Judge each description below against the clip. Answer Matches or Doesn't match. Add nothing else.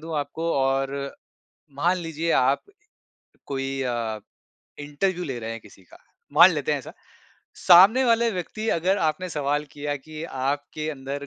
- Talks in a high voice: Doesn't match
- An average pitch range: Matches